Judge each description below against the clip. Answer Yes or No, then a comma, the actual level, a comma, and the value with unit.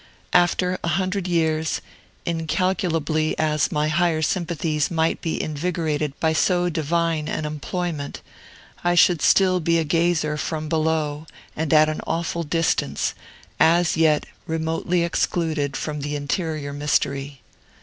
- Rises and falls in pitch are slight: Yes, narrow, 2.0 semitones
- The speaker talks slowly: Yes, slow, 130 wpm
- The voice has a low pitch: No, medium, 160 Hz